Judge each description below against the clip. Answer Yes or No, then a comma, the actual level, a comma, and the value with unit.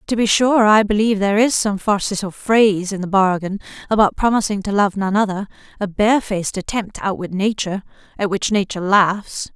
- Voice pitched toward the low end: No, high, 200 Hz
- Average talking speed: Yes, average, 175 wpm